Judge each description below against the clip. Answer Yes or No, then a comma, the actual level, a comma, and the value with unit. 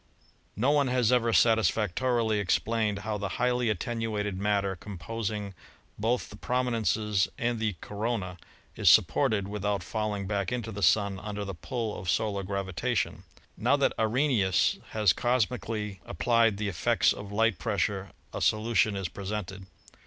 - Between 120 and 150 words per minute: Yes, average, 140 wpm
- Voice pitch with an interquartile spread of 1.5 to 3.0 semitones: Yes, narrow, 2.5 semitones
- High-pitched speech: No, low, 105 Hz